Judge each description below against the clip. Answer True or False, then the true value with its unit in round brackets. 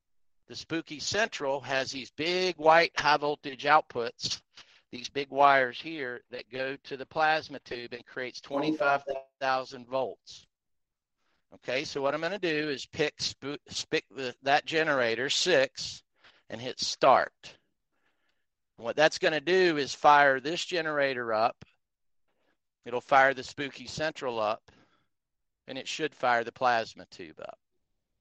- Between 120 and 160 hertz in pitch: True (140 Hz)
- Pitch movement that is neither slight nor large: True (3.2 semitones)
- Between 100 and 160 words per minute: True (140 wpm)